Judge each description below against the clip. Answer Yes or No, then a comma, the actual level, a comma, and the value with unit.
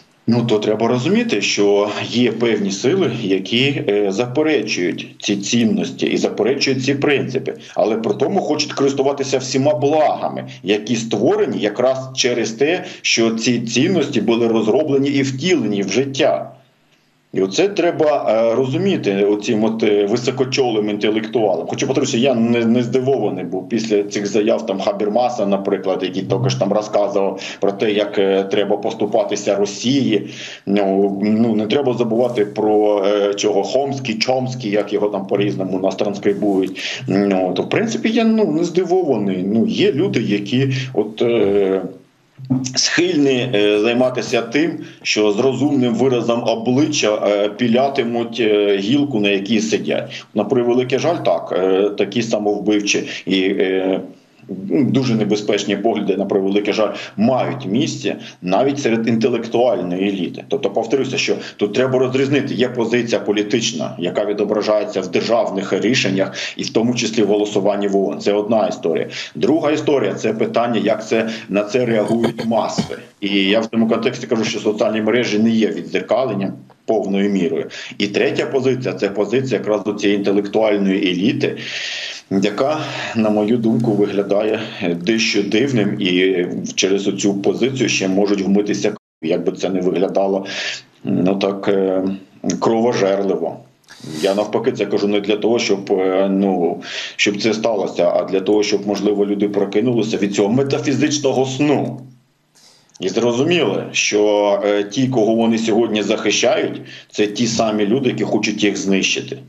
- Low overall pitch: Yes, low, 105 Hz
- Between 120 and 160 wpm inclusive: Yes, average, 140 wpm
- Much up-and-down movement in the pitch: No, average, 3.7 semitones